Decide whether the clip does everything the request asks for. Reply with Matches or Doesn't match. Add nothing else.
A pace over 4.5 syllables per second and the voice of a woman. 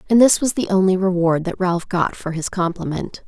Matches